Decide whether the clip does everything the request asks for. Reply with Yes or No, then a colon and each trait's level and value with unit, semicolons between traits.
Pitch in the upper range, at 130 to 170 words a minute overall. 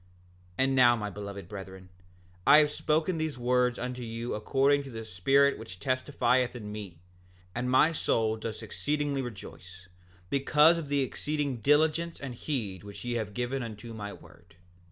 No: low, 125 Hz; average, 165 wpm